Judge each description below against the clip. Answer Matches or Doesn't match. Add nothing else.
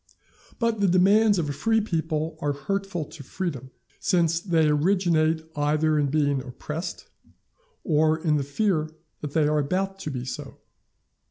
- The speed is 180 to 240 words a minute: Doesn't match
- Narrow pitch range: Doesn't match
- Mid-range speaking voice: Matches